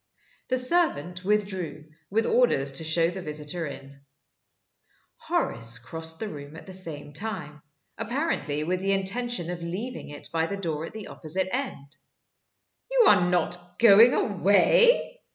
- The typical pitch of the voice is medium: Yes, medium, 180 Hz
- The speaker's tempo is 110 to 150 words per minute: Yes, average, 145 wpm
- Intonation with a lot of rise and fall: Yes, wide, 6.2 semitones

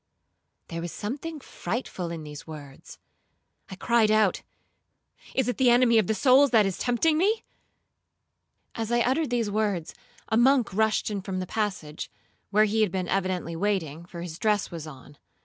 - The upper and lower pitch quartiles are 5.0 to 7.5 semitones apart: Yes, wide, 5.5 semitones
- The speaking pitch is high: Yes, high, 210 Hz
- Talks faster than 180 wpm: No, average, 165 wpm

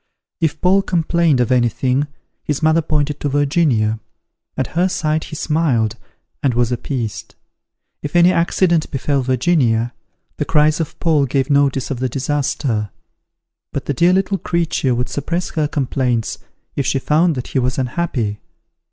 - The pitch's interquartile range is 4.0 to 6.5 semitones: Yes, average, 4.4 semitones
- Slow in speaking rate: No, average, 150 wpm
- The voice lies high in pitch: No, medium, 145 Hz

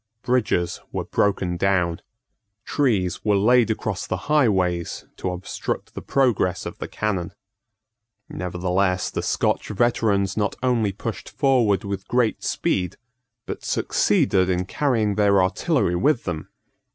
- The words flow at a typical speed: No, slow, 125 wpm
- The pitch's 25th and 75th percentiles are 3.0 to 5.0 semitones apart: Yes, average, 4.0 semitones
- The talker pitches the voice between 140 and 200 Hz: No, low, 100 Hz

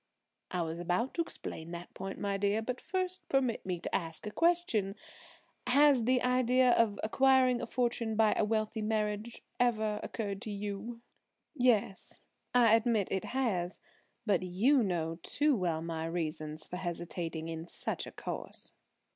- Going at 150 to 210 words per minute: Yes, average, 155 wpm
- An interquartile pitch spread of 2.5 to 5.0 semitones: No, wide, 5.5 semitones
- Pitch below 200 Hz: No, high, 215 Hz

